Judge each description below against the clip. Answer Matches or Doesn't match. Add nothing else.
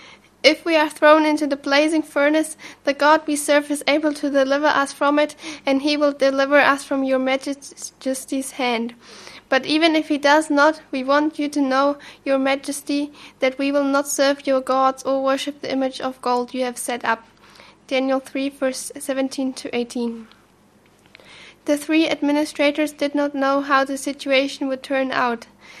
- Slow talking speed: Doesn't match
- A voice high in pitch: Matches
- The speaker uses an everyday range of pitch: Doesn't match